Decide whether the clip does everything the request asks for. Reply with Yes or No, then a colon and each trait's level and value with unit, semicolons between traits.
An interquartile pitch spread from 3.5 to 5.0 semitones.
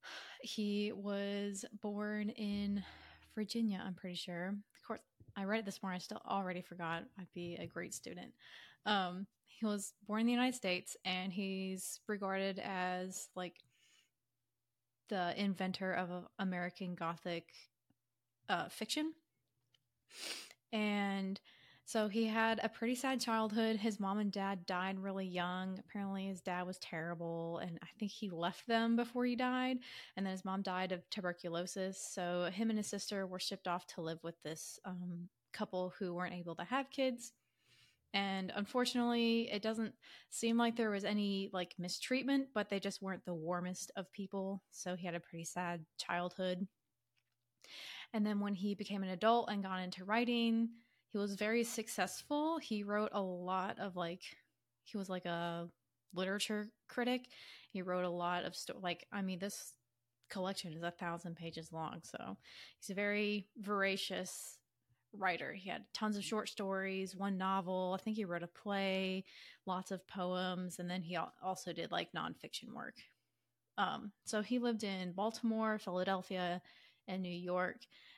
No: average, 2.9 semitones